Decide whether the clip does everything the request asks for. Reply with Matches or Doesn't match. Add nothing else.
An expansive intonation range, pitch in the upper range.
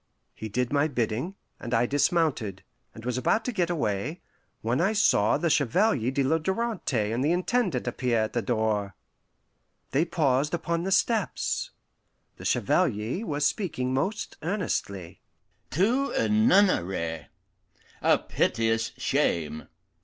Doesn't match